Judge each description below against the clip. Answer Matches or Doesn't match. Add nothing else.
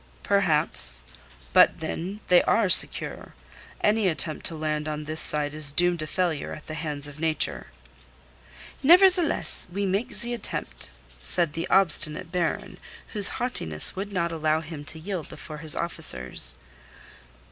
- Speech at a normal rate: Matches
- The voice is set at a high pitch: Doesn't match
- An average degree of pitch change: Matches